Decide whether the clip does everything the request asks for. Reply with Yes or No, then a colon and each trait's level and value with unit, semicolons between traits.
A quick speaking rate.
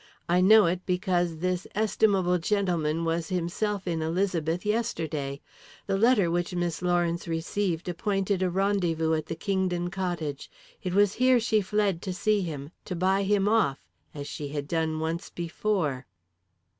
No: average, 155 wpm